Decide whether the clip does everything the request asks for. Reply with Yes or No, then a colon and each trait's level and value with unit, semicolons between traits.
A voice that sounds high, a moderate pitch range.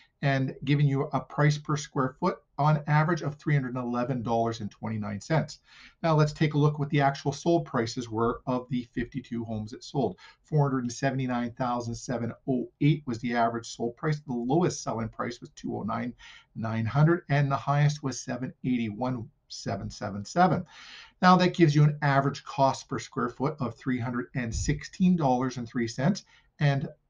No: low, 135 Hz; average, 3.8 semitones